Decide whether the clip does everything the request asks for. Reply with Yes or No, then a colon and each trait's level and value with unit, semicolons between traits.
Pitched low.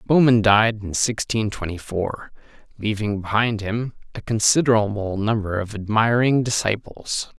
Yes: low, 110 Hz